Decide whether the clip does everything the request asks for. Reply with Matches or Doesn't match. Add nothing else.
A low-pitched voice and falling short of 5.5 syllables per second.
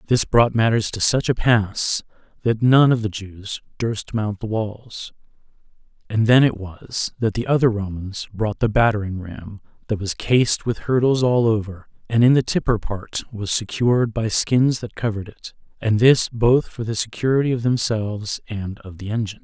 Matches